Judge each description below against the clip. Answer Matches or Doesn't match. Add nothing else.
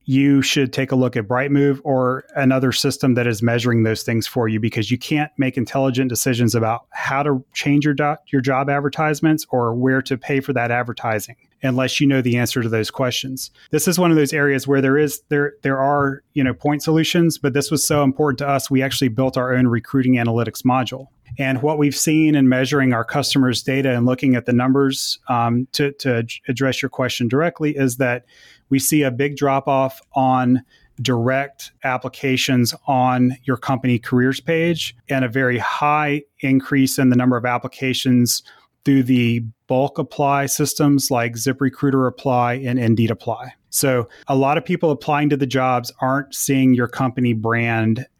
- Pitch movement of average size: Doesn't match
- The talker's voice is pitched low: Matches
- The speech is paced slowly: Doesn't match